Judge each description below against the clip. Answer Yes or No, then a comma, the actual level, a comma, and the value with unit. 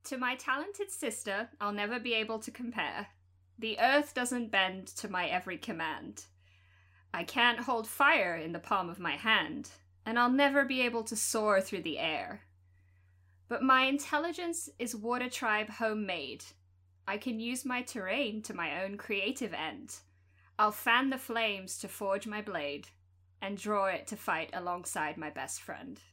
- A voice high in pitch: Yes, high, 210 Hz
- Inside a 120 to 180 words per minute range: Yes, average, 165 wpm